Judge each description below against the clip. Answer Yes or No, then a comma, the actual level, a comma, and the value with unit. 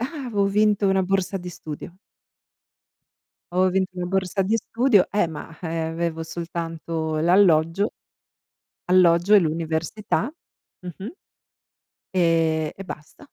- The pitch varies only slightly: No, average, 3.2 semitones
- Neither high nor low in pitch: Yes, medium, 180 Hz